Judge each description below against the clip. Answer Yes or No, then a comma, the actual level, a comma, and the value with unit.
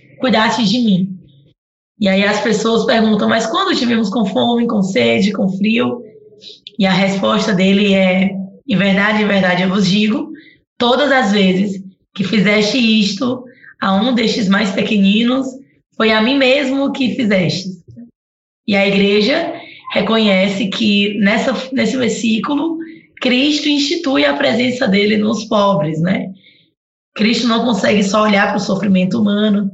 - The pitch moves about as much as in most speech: Yes, average, 3.6 semitones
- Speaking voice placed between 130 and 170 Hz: No, high, 215 Hz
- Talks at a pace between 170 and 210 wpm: No, average, 145 wpm